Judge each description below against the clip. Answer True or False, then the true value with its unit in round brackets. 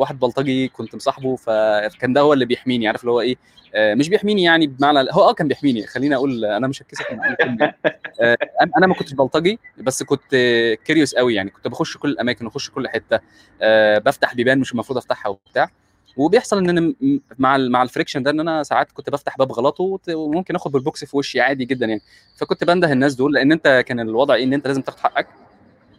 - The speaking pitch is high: False (135 Hz)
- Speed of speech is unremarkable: False (200 wpm)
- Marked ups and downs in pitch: False (4.3 semitones)